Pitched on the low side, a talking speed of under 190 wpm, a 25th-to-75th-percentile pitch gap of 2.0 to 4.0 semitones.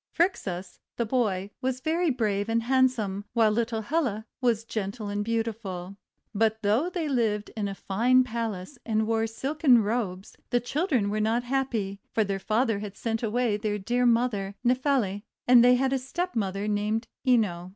No: high, 225 Hz; average, 165 wpm; average, 3.4 semitones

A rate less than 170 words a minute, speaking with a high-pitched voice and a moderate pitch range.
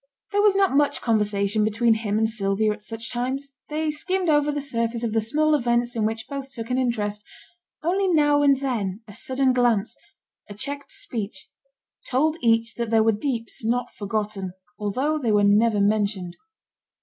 No: average, 175 wpm; high, 230 Hz; average, 4.8 semitones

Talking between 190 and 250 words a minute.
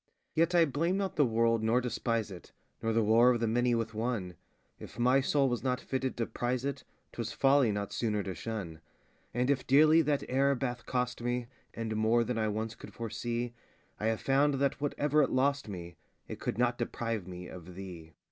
Yes: fast, 205 wpm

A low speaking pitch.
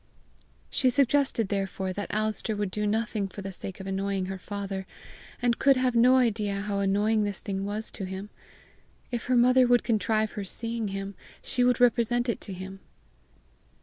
No: high, 210 Hz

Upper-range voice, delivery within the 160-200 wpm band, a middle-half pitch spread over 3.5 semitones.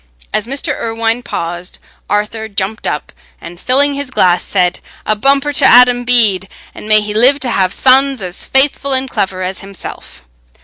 Yes: high, 225 Hz; average, 170 wpm; wide, 5.4 semitones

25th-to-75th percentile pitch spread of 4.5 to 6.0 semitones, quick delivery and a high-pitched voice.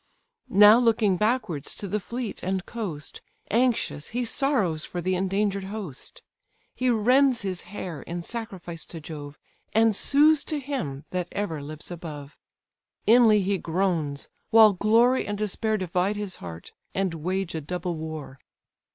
No: average, 5.1 semitones; average, 145 wpm; high, 195 Hz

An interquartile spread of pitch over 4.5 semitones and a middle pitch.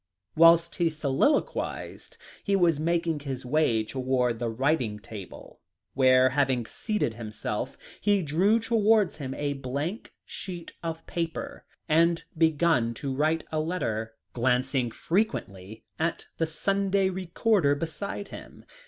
Yes: average, 5.1 semitones; medium, 155 Hz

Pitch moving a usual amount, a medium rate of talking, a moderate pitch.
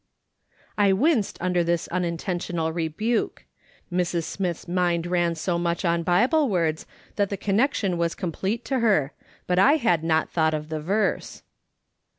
Yes: average, 3.1 semitones; average, 150 wpm; medium, 175 Hz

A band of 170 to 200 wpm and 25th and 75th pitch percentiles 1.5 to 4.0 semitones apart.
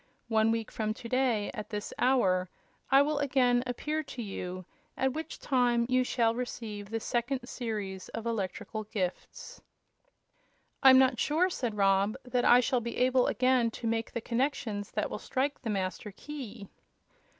No: average, 160 wpm; average, 3.4 semitones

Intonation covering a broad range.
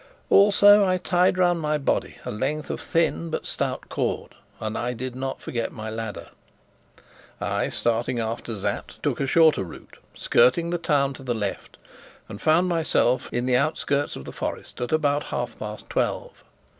Yes: wide, 5.7 semitones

